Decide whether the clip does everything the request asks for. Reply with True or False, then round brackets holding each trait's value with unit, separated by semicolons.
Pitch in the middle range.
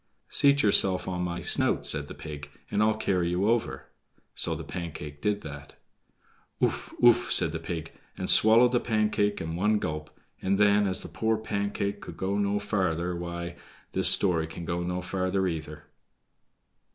False (95 Hz)